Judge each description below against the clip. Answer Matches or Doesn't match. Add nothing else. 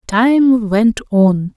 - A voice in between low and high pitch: Doesn't match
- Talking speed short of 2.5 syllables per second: Matches